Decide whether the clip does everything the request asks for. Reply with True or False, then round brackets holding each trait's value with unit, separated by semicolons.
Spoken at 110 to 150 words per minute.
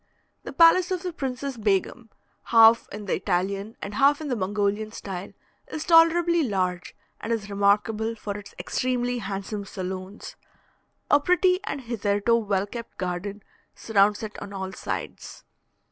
True (145 wpm)